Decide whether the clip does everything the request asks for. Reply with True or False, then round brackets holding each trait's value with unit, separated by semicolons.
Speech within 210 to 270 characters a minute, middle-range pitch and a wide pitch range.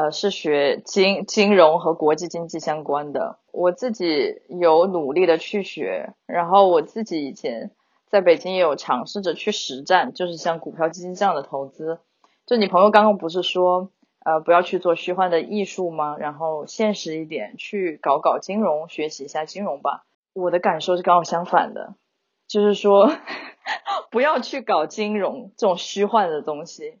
False (260 characters per minute; 180 Hz; 4.3 semitones)